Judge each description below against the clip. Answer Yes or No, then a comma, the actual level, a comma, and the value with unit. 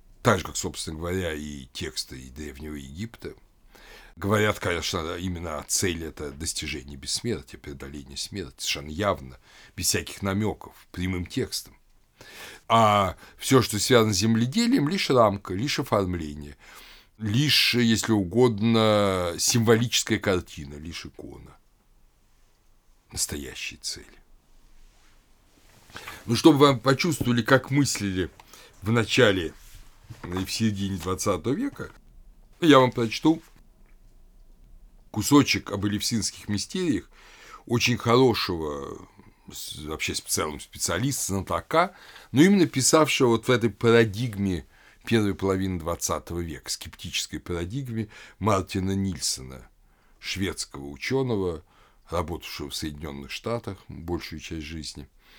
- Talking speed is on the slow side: Yes, slow, 105 wpm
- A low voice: Yes, low, 100 Hz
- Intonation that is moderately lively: No, wide, 5.9 semitones